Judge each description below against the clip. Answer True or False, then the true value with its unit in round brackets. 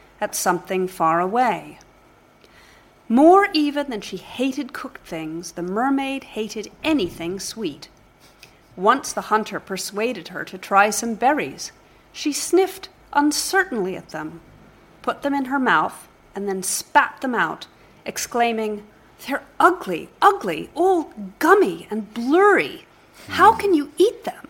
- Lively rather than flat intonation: True (7.8 semitones)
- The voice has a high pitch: True (235 Hz)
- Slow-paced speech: True (130 wpm)